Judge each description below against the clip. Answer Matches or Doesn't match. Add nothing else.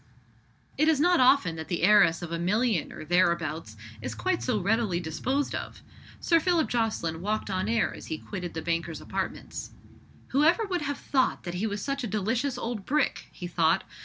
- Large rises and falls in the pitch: Matches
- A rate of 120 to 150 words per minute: Doesn't match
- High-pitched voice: Matches